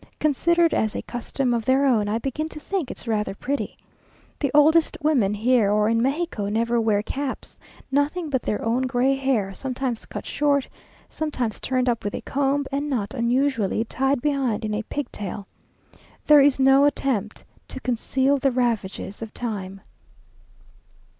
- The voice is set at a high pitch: Yes, very high, 255 Hz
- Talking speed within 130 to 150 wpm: No, average, 160 wpm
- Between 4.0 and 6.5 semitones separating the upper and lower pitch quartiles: Yes, average, 4.3 semitones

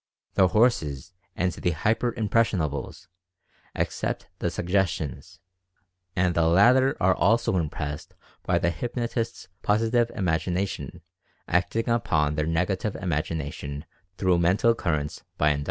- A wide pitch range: Yes, wide, 5.8 semitones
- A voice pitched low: Yes, very low, 90 Hz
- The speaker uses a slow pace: Yes, slow, 115 wpm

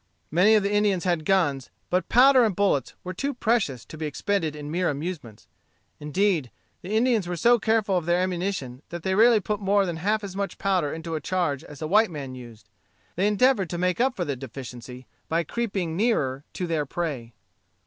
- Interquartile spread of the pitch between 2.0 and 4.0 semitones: No, wide, 5.5 semitones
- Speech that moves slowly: No, average, 200 wpm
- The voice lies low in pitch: No, medium, 180 Hz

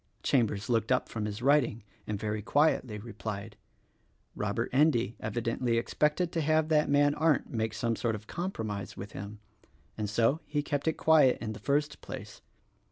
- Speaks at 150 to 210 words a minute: Yes, average, 165 wpm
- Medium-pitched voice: No, low, 120 Hz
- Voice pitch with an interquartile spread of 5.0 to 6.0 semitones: Yes, wide, 5.4 semitones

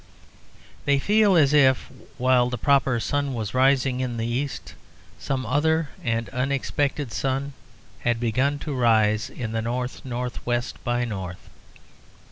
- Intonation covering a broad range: No, average, 2.9 semitones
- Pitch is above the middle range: No, low, 130 Hz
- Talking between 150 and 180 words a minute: No, average, 140 wpm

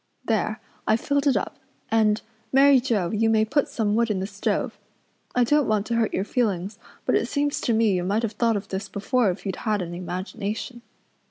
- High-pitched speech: Yes, high, 220 Hz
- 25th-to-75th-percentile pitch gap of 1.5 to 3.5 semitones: Yes, average, 3.1 semitones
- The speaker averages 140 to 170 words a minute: No, fast, 205 wpm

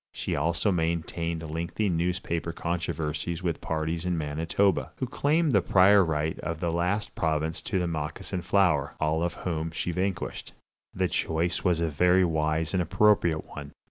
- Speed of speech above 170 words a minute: No, average, 155 wpm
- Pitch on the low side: Yes, very low, 85 Hz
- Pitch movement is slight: Yes, narrow, 2.3 semitones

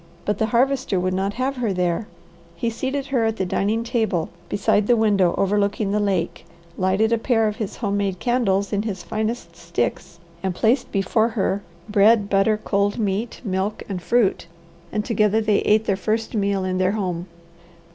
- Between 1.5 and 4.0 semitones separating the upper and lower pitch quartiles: Yes, narrow, 2.6 semitones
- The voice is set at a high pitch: Yes, high, 205 Hz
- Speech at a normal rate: Yes, average, 180 wpm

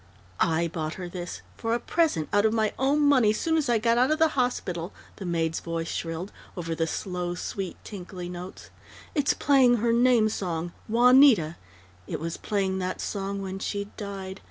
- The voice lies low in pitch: No, high, 195 Hz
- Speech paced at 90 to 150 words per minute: No, average, 180 wpm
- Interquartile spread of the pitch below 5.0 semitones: No, wide, 5.5 semitones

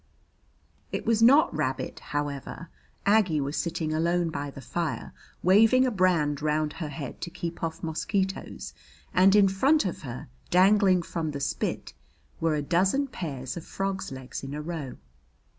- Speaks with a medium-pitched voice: Yes, medium, 170 Hz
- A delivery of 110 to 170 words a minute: Yes, average, 160 wpm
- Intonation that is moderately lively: Yes, average, 4.6 semitones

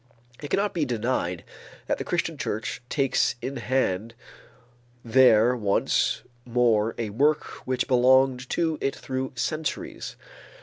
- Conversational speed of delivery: No, slow, 125 wpm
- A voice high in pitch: No, low, 125 Hz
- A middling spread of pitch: Yes, average, 3.0 semitones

